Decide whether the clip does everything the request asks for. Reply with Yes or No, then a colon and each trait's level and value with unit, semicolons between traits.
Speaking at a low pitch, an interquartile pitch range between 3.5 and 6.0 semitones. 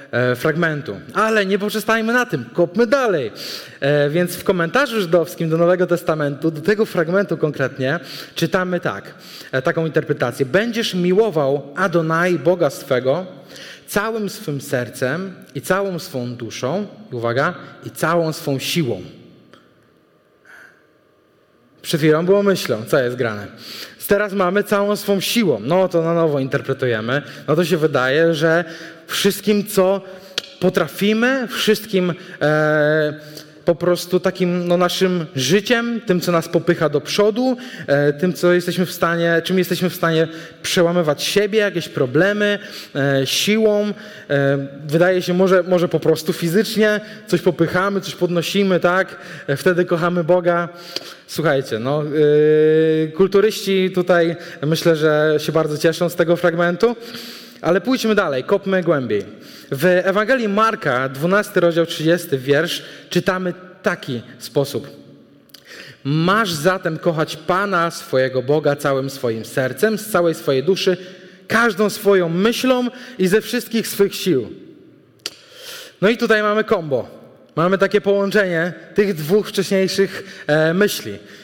No: medium, 175 Hz; average, 4.6 semitones